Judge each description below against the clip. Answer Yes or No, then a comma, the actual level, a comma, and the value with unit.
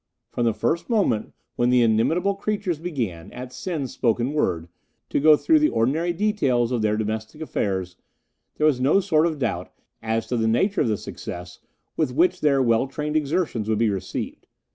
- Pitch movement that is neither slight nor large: No, wide, 6.6 semitones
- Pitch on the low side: Yes, low, 130 Hz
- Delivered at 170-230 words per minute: Yes, average, 185 wpm